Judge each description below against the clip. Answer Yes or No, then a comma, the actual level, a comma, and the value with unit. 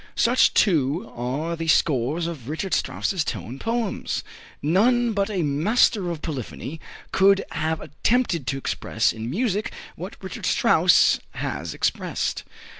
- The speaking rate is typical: No, slow, 130 wpm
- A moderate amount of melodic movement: No, wide, 6.1 semitones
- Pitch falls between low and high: Yes, medium, 165 Hz